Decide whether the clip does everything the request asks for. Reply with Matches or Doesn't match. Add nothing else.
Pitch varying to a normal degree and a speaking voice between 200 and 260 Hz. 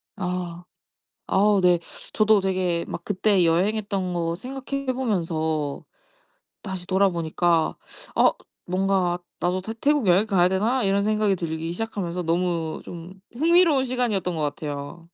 Doesn't match